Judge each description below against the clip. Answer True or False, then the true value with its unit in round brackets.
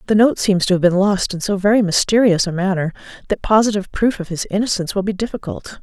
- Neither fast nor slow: False (225 wpm)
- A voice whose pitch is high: True (200 Hz)